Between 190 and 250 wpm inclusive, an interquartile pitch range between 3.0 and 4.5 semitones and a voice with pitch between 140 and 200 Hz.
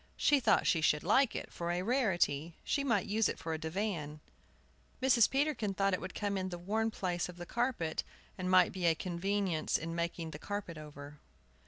Yes: average, 200 wpm; average, 4.0 semitones; medium, 185 Hz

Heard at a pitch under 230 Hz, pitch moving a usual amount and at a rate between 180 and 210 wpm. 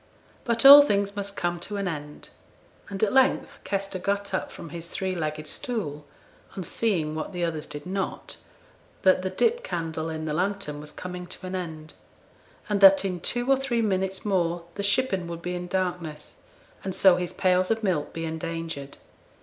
Yes: medium, 185 Hz; average, 3.5 semitones; average, 185 wpm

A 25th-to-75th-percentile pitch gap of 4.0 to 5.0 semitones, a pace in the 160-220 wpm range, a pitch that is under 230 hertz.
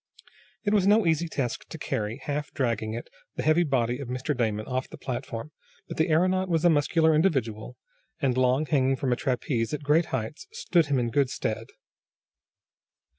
Yes: average, 4.7 semitones; average, 180 wpm; medium, 140 Hz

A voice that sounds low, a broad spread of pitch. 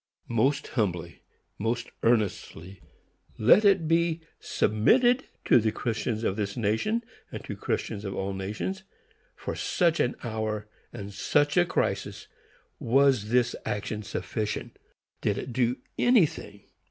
Yes: low, 115 Hz; wide, 6.8 semitones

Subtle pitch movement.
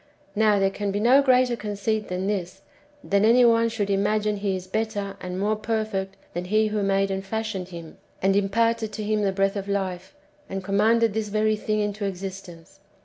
Yes: narrow, 1.9 semitones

